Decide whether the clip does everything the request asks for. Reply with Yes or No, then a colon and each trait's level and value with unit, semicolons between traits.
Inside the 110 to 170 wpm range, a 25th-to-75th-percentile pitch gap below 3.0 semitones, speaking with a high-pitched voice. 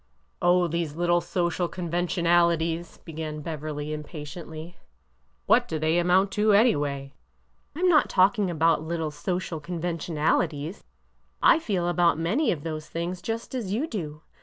No: average, 150 wpm; narrow, 2.6 semitones; medium, 170 Hz